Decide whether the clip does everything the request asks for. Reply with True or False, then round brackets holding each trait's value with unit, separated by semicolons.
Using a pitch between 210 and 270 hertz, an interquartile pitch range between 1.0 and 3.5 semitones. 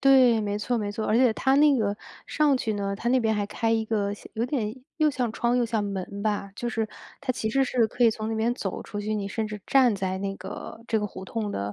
True (220 Hz; 3.0 semitones)